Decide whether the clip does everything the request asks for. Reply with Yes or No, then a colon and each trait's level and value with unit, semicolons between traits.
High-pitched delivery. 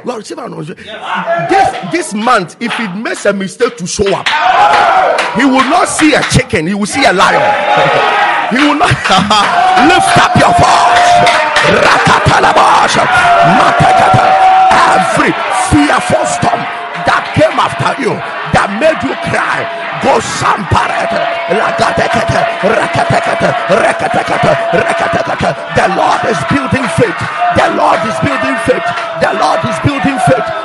Yes: very high, 275 Hz